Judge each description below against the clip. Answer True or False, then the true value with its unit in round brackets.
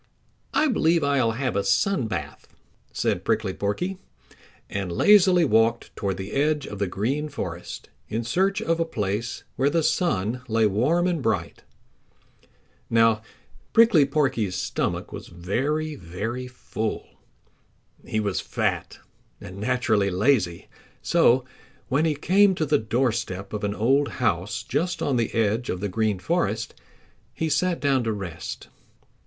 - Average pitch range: False (6.7 semitones)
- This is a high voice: False (115 Hz)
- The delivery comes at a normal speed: True (145 wpm)